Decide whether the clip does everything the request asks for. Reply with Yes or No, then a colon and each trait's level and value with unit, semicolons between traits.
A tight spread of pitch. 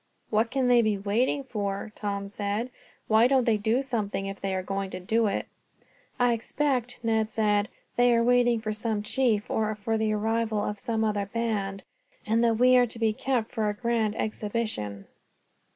Yes: narrow, 2.2 semitones